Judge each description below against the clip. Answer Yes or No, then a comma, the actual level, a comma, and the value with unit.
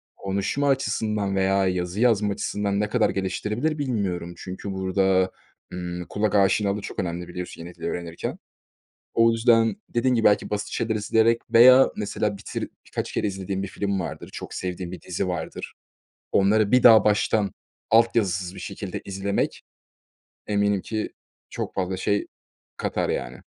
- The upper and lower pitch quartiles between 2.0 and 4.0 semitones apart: Yes, average, 2.7 semitones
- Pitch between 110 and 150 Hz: No, low, 100 Hz